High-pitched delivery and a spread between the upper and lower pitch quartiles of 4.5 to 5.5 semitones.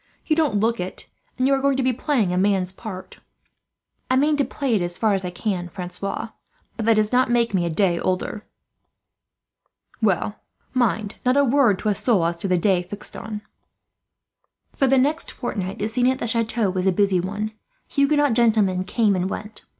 Yes: high, 215 Hz; average, 5.0 semitones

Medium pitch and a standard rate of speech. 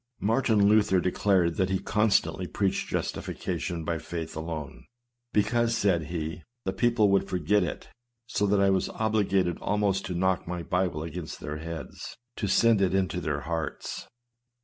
No: very low, 95 Hz; average, 160 wpm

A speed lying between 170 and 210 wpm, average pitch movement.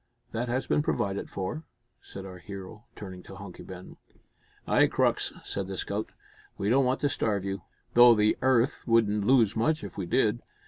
Yes: average, 180 wpm; average, 3.8 semitones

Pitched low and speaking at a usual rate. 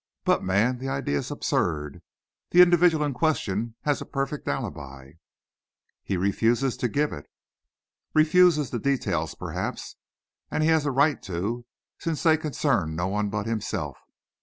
Yes: low, 125 Hz; average, 150 wpm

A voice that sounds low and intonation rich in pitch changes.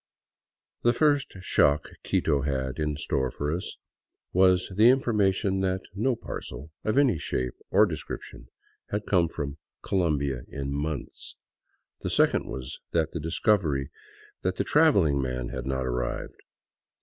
Yes: very low, 80 Hz; wide, 6.4 semitones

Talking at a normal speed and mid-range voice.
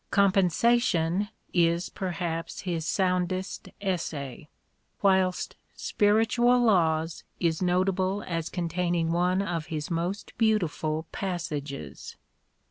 No: slow, 110 wpm; medium, 180 Hz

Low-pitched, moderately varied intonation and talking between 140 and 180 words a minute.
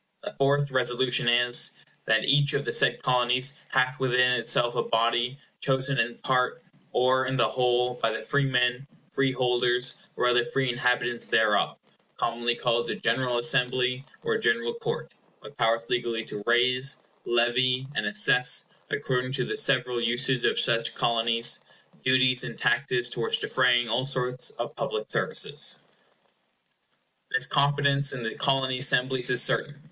No: low, 125 Hz; narrow, 1.6 semitones; average, 150 wpm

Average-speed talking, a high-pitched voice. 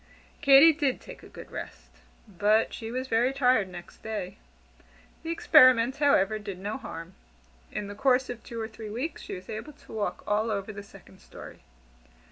Yes: average, 180 wpm; high, 225 Hz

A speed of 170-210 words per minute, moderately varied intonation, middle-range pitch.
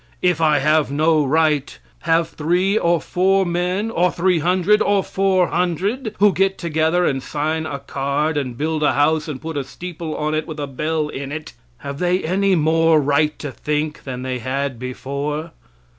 Yes: average, 175 wpm; average, 3.4 semitones; medium, 155 Hz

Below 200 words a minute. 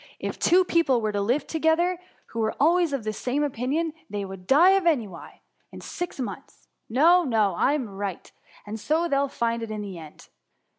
No: fast, 205 wpm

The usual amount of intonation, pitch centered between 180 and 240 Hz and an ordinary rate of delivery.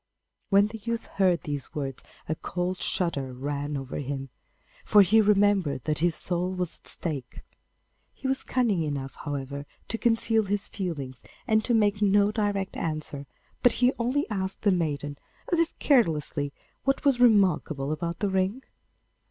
No: wide, 6.4 semitones; medium, 185 Hz; average, 160 wpm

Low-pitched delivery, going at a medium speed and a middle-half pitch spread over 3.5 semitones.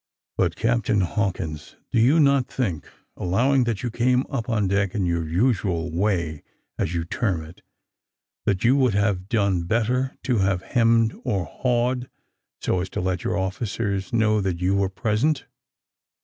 Yes: low, 100 Hz; average, 165 wpm; average, 4.6 semitones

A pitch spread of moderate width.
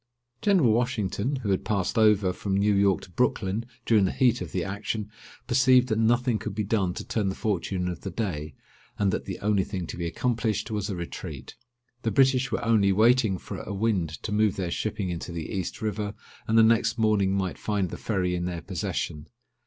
Yes: average, 3.1 semitones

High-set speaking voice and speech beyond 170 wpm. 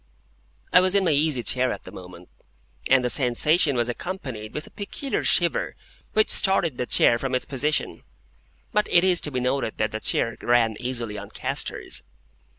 No: low, 130 Hz; average, 180 wpm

